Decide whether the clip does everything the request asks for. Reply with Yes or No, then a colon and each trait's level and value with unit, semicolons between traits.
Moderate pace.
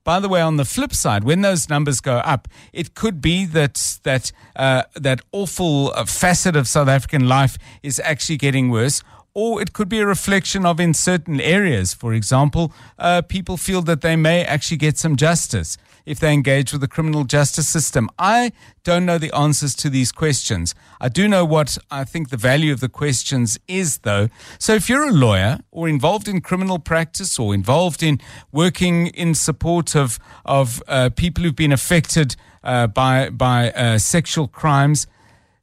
Yes: average, 185 wpm